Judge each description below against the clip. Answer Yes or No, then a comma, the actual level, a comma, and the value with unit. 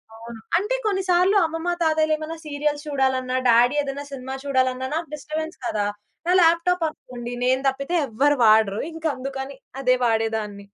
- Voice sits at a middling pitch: No, very high, 275 Hz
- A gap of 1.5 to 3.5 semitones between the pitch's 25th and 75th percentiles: No, average, 4.1 semitones